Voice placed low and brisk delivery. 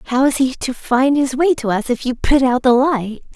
No: very high, 260 Hz; fast, 270 wpm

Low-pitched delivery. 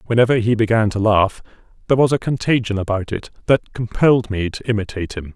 Yes: low, 110 Hz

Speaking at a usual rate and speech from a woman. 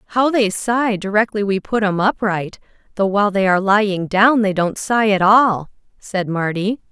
Yes: average, 180 wpm; female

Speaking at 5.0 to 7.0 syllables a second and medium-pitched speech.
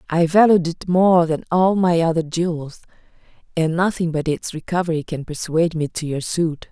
Yes: 5.1 syllables/s; medium, 165 Hz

